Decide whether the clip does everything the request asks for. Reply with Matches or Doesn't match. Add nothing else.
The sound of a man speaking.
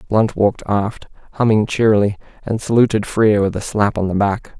Matches